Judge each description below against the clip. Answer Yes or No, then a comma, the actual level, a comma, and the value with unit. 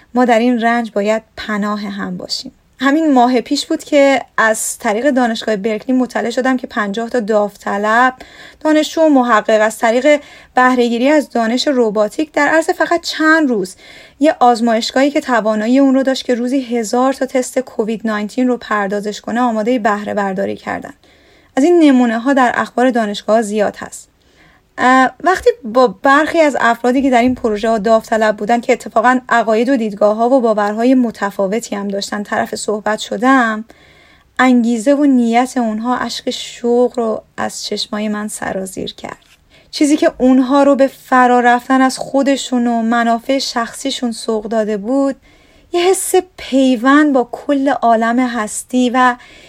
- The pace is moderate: No, fast, 160 wpm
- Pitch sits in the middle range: No, high, 245 Hz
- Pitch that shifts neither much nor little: Yes, average, 3.3 semitones